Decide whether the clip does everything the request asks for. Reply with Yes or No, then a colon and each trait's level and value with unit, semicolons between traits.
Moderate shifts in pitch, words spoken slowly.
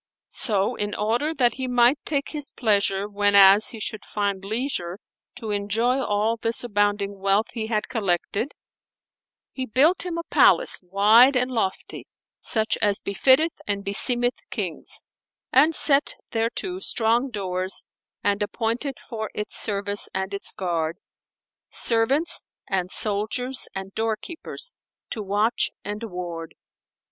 Yes: average, 3.8 semitones; slow, 130 wpm